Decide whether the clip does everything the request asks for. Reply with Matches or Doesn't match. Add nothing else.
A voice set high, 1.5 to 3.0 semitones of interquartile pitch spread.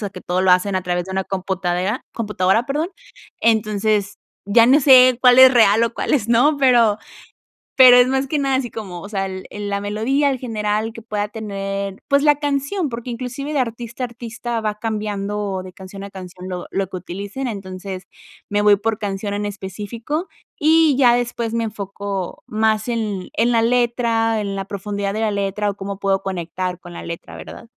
Doesn't match